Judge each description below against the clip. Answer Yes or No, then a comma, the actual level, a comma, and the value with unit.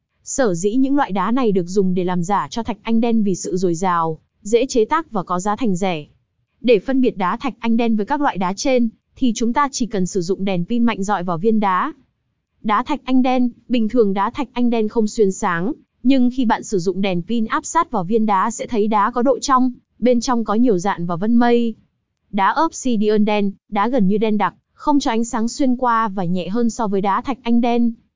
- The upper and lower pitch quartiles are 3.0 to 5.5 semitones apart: Yes, average, 4.0 semitones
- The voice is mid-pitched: No, high, 225 Hz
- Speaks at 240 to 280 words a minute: Yes, average, 245 wpm